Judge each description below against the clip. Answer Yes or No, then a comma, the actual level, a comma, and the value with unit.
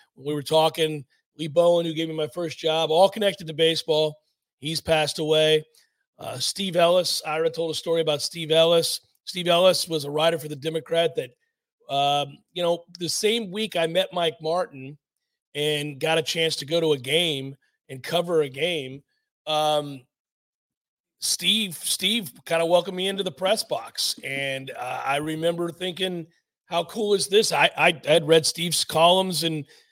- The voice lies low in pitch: No, medium, 165 Hz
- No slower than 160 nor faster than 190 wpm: Yes, average, 175 wpm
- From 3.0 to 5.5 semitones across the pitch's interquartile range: No, narrow, 2.5 semitones